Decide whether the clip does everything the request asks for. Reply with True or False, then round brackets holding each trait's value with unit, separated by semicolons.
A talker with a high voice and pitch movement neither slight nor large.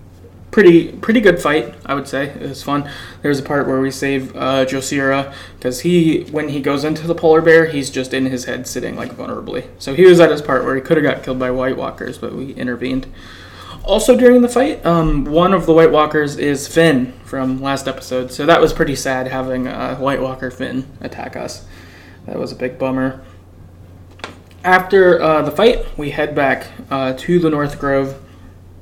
False (135 Hz; 3.8 semitones)